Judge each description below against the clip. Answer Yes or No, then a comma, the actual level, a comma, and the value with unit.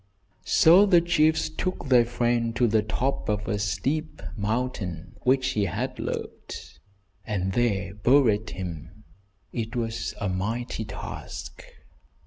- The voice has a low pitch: Yes, low, 115 Hz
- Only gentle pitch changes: No, average, 4.1 semitones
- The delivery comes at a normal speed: No, slow, 125 wpm